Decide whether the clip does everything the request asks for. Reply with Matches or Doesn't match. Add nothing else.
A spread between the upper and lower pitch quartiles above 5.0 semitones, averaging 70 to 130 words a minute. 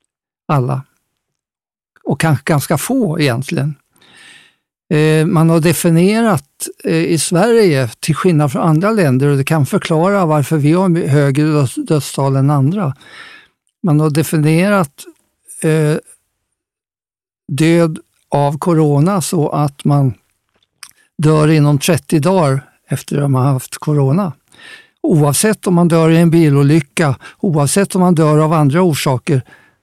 Doesn't match